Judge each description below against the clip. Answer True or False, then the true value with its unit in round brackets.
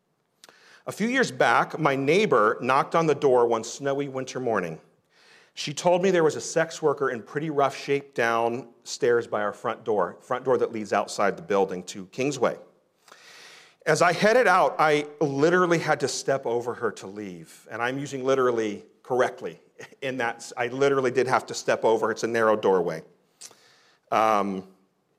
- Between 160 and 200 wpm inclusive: True (175 wpm)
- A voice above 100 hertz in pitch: True (140 Hz)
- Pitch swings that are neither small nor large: False (5.9 semitones)